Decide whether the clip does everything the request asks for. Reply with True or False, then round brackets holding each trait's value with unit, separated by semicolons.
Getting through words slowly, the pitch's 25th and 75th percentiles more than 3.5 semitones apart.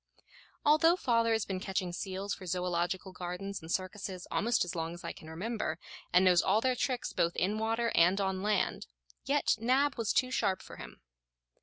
False (185 wpm; 4.2 semitones)